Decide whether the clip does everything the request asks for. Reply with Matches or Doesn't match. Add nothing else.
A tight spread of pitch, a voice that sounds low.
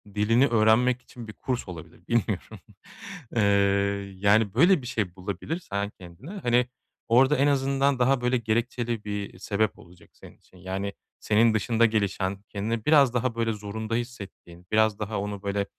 Doesn't match